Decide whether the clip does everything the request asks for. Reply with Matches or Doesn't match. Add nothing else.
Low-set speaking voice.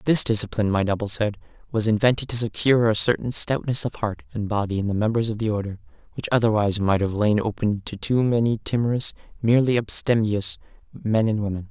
Matches